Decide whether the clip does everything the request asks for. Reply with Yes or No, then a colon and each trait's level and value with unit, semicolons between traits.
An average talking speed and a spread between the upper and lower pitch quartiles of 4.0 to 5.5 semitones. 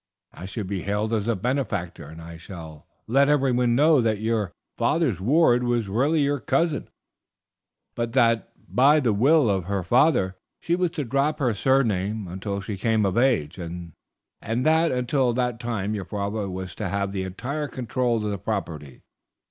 Yes: average, 170 wpm; average, 5.2 semitones